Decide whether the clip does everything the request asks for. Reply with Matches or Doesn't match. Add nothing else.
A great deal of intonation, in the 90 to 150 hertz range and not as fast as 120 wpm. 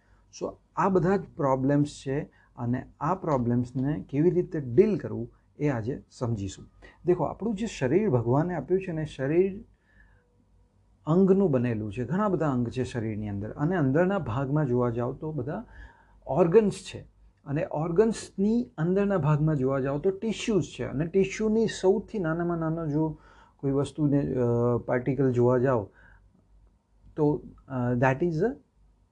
Doesn't match